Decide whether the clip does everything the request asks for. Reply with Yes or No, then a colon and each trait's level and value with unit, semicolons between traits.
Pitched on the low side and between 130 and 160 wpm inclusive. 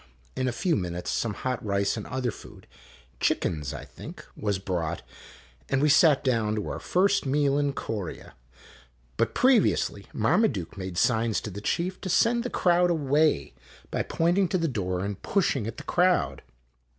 No: low, 130 Hz; average, 180 wpm